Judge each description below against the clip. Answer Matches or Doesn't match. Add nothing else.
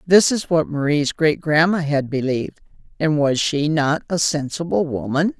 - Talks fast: Doesn't match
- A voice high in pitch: Doesn't match